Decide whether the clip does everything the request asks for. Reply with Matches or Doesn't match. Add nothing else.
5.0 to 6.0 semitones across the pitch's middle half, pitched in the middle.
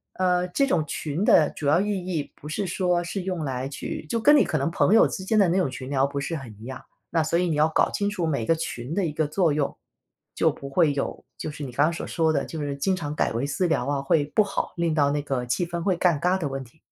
Doesn't match